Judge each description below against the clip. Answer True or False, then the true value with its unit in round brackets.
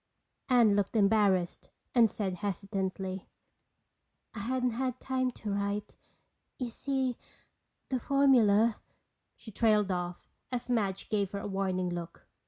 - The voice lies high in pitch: True (210 Hz)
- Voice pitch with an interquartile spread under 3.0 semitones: False (3.9 semitones)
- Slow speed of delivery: True (125 wpm)